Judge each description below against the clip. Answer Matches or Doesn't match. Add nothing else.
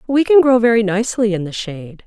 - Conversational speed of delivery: Doesn't match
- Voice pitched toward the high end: Matches